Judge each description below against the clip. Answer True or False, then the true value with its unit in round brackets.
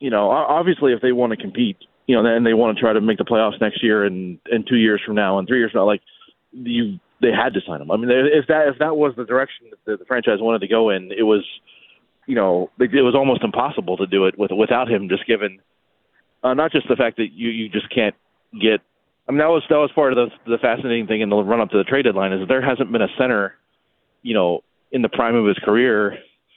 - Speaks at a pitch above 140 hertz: False (115 Hz)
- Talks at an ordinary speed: False (265 wpm)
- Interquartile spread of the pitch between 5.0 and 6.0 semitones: True (5.5 semitones)